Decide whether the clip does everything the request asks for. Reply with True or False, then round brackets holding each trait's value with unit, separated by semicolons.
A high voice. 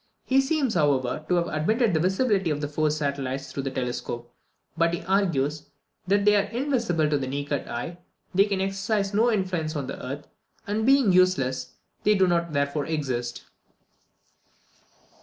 False (170 Hz)